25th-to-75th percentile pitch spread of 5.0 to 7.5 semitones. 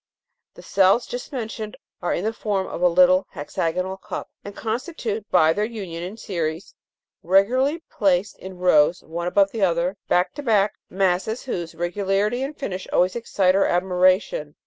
No: average, 3.4 semitones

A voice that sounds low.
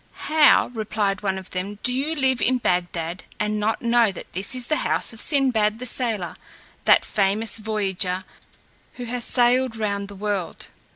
No: high, 215 Hz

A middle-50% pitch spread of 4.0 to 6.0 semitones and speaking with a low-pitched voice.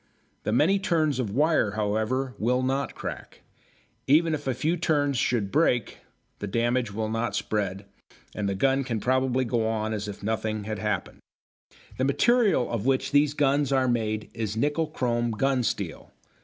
Yes: average, 4.4 semitones; low, 125 Hz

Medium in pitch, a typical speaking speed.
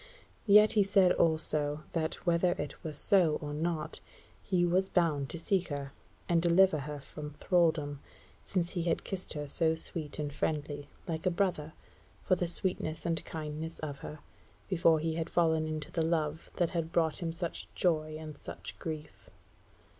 Yes: medium, 160 Hz; average, 170 wpm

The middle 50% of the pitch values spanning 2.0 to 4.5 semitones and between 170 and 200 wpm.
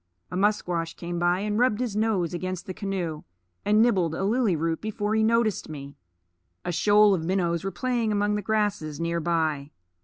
Yes: average, 3.9 semitones; average, 185 wpm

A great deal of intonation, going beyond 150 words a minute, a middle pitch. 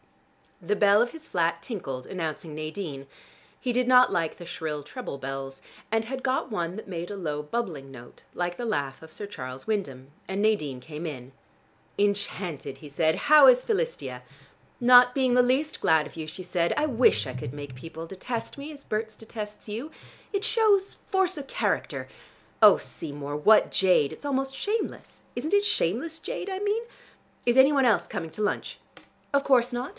No: wide, 8.7 semitones; average, 185 wpm; high, 205 Hz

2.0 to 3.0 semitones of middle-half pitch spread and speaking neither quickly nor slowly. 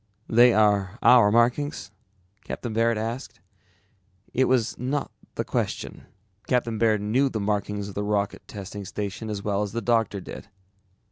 Yes: narrow, 2.6 semitones; average, 150 wpm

